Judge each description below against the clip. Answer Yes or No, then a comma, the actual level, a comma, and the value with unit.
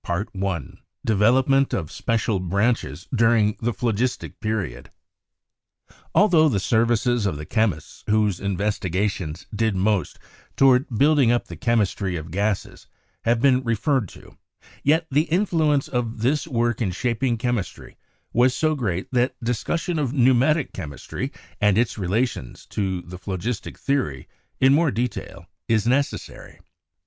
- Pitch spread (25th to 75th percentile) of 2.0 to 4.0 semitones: No, average, 4.8 semitones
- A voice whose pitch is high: No, low, 115 Hz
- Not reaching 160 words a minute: Yes, average, 140 wpm